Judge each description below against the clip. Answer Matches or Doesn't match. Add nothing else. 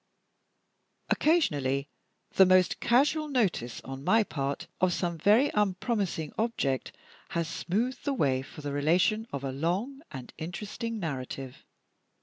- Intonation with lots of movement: Matches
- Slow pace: Matches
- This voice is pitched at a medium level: Matches